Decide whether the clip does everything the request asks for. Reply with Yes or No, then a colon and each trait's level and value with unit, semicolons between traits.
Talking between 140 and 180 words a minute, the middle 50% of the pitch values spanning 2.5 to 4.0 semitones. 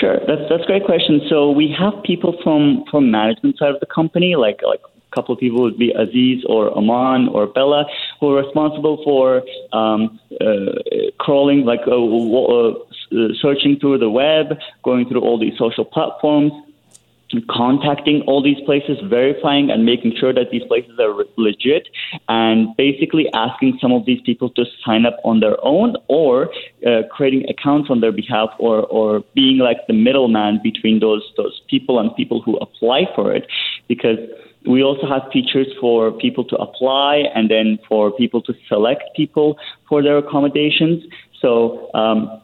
No: average, 170 wpm; average, 4.4 semitones